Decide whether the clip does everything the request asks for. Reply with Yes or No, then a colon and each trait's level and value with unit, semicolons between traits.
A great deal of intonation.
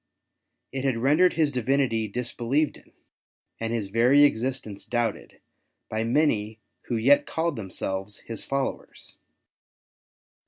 No: average, 3.7 semitones